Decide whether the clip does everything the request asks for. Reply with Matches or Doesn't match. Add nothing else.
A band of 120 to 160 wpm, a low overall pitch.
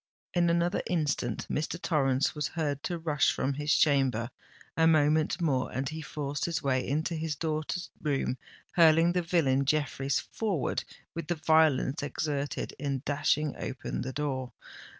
Doesn't match